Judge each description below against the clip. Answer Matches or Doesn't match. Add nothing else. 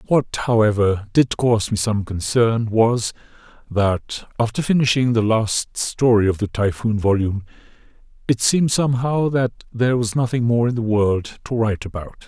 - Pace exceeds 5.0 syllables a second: Doesn't match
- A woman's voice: Doesn't match